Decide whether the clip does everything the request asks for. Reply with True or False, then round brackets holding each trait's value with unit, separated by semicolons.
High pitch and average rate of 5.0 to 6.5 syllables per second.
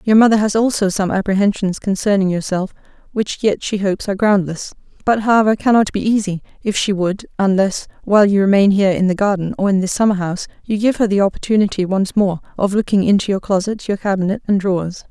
True (200 Hz; 5.1 syllables/s)